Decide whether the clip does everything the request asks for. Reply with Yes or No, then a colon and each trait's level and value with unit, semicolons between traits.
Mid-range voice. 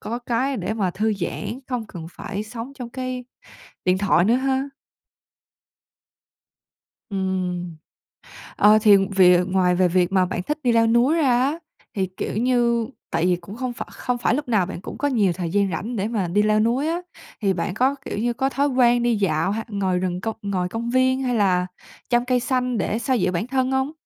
No: high, 225 Hz